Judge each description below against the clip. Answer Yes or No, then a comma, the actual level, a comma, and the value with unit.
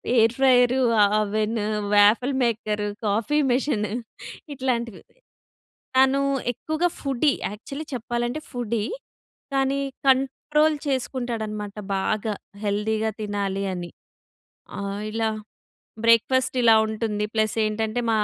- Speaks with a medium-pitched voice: No, high, 230 Hz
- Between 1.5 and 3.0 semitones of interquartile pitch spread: No, average, 3.6 semitones